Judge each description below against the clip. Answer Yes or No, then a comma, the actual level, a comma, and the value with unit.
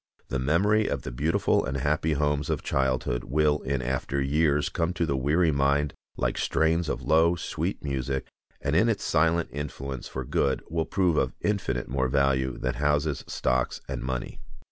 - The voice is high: No, very low, 70 Hz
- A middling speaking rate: Yes, average, 175 wpm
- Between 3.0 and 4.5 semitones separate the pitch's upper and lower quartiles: Yes, average, 3.3 semitones